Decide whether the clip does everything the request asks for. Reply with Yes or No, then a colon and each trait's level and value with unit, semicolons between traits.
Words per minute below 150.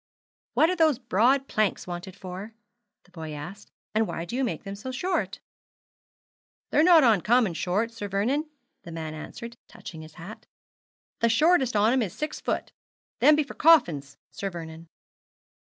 No: average, 165 wpm